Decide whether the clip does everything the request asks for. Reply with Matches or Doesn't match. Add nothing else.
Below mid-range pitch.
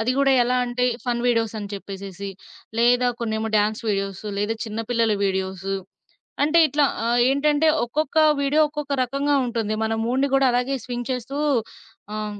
Doesn't match